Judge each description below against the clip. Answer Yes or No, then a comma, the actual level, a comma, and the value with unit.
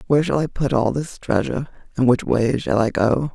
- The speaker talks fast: Yes, fast, 235 wpm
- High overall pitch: No, low, 130 Hz